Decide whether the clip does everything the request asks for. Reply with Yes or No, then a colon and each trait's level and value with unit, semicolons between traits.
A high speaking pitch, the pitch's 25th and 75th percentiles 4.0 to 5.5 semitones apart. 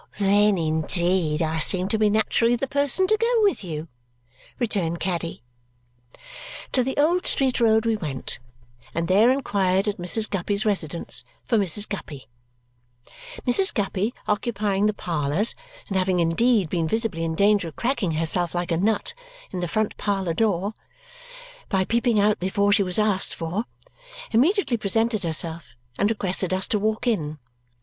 Yes: high, 200 Hz; average, 4.5 semitones